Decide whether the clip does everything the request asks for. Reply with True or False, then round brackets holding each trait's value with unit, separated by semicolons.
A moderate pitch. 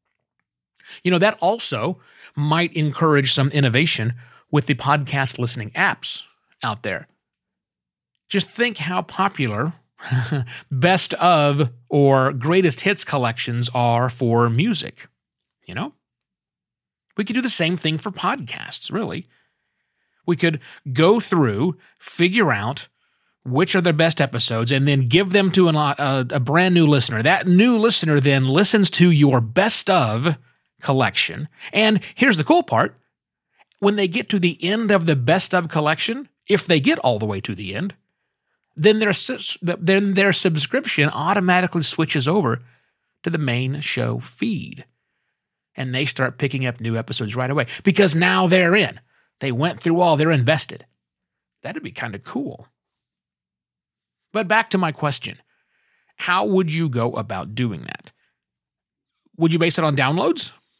True (155 Hz)